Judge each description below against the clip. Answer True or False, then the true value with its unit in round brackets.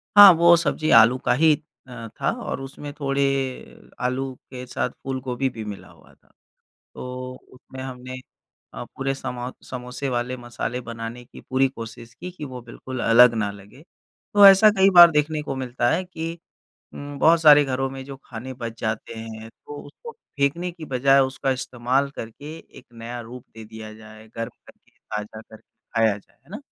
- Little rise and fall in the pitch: False (3.5 semitones)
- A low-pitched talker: True (130 Hz)